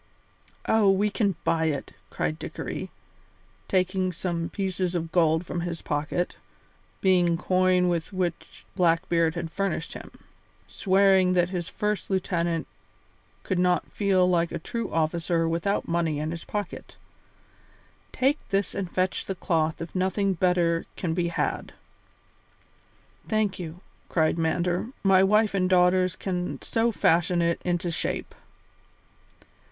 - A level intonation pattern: Yes, narrow, 2.2 semitones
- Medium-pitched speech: Yes, medium, 180 Hz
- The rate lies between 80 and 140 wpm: Yes, slow, 135 wpm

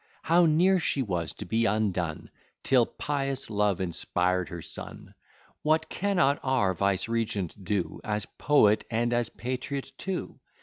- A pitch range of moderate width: No, wide, 6.4 semitones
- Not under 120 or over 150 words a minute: Yes, slow, 135 wpm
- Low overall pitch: Yes, low, 110 Hz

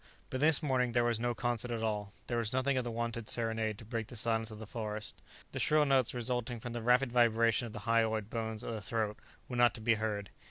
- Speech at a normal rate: No, fast, 245 wpm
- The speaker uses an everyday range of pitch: No, narrow, 1.7 semitones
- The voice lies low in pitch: Yes, low, 115 Hz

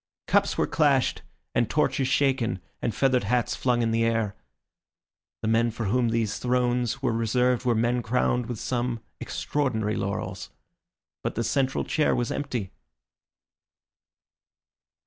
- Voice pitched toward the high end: No, low, 120 Hz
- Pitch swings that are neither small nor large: No, narrow, 2.0 semitones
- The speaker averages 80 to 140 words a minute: Yes, slow, 135 wpm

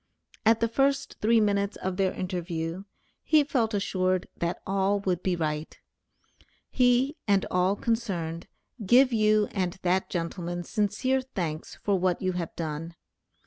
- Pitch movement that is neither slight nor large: Yes, average, 4.1 semitones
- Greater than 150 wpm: No, average, 145 wpm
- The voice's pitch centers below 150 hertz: No, high, 190 Hz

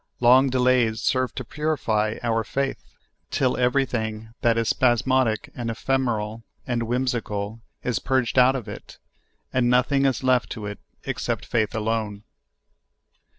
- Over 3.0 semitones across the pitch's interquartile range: No, narrow, 2.6 semitones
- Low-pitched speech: Yes, low, 120 Hz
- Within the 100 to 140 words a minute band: Yes, slow, 135 wpm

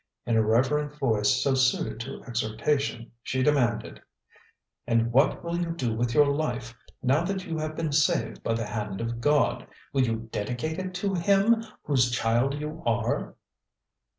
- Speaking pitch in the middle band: No, low, 130 Hz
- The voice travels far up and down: No, average, 4.8 semitones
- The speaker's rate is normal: Yes, average, 165 wpm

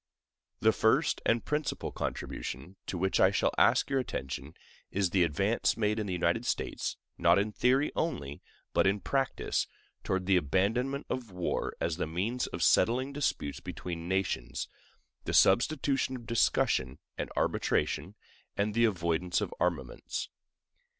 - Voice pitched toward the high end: No, low, 100 Hz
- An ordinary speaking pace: Yes, average, 145 wpm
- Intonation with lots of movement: Yes, wide, 6.1 semitones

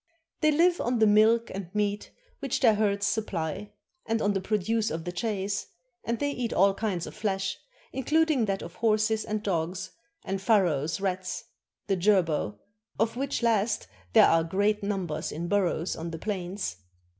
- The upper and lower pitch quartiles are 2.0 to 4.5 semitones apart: Yes, average, 3.4 semitones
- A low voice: No, high, 205 Hz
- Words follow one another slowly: No, average, 165 wpm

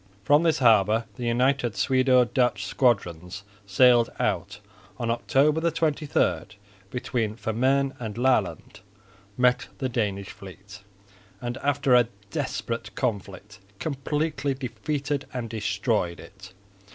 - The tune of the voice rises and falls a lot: No, average, 4.4 semitones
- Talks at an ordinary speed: No, slow, 115 wpm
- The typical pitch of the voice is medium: No, low, 120 Hz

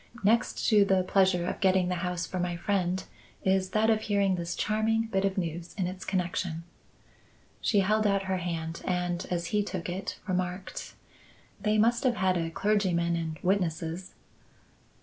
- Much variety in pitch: No, narrow, 2.5 semitones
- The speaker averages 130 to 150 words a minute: No, average, 165 wpm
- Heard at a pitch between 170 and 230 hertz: Yes, medium, 185 Hz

